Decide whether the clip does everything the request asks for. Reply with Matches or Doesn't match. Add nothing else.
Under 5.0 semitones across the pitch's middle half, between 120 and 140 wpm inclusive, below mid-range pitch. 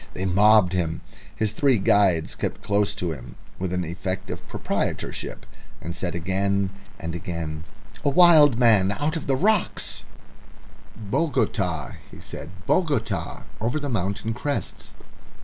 Doesn't match